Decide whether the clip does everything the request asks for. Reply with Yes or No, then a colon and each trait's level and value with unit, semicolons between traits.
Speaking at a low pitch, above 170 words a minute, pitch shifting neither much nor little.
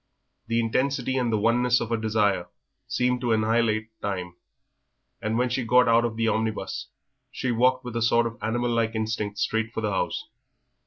No: low, 115 Hz; average, 180 wpm; narrow, 1.9 semitones